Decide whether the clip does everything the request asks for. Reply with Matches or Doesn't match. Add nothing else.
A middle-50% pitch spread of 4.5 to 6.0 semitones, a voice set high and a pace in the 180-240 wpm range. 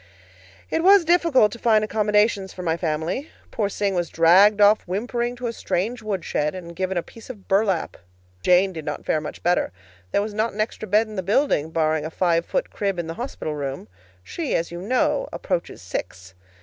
Matches